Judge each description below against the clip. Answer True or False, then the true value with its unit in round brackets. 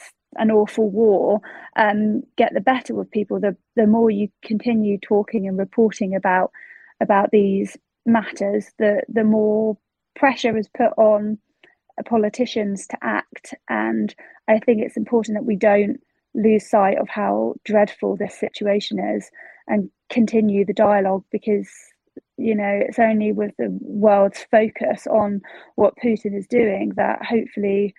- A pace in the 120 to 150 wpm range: True (145 wpm)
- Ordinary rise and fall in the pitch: False (2.2 semitones)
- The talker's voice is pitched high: True (215 Hz)